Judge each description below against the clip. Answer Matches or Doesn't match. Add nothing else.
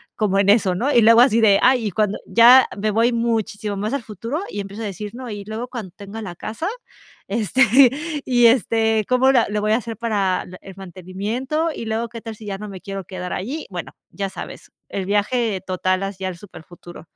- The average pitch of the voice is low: Doesn't match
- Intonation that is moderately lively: Matches